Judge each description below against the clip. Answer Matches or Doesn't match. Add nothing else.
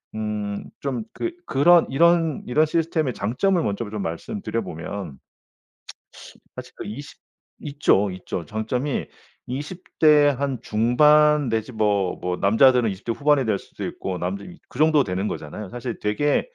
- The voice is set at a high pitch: Doesn't match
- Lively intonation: Matches